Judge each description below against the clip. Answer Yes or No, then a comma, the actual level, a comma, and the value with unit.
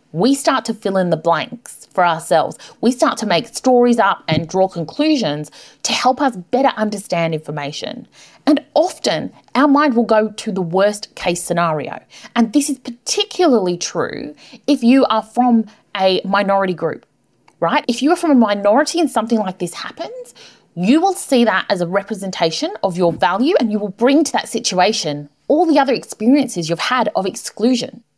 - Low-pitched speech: No, high, 220 Hz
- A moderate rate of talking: Yes, average, 180 wpm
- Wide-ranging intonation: Yes, wide, 6.8 semitones